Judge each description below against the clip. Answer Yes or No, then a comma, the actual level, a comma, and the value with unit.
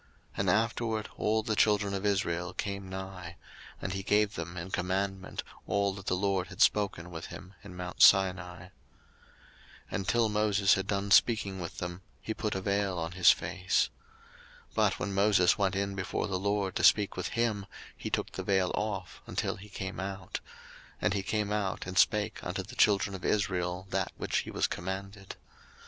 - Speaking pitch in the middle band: No, very low, 95 Hz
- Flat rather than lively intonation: Yes, narrow, 1.9 semitones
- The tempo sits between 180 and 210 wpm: Yes, average, 190 wpm